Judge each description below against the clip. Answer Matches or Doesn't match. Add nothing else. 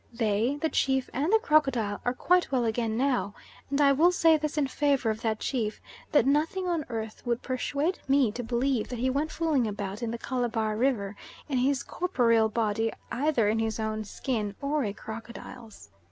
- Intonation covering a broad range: Doesn't match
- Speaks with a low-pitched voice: Doesn't match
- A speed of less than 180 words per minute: Doesn't match